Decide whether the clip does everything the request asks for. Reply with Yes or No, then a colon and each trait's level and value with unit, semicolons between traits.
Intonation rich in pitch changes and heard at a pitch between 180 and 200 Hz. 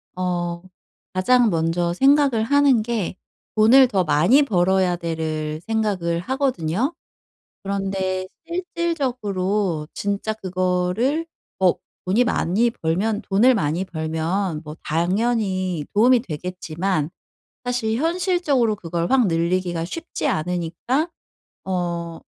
Yes: wide, 5.8 semitones; high, 190 Hz